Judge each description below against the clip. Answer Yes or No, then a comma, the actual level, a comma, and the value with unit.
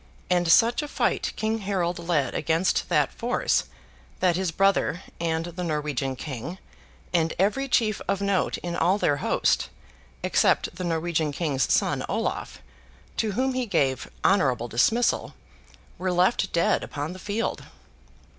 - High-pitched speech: No, medium, 175 Hz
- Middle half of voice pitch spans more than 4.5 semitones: No, average, 4.0 semitones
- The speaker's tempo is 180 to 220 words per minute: No, average, 145 wpm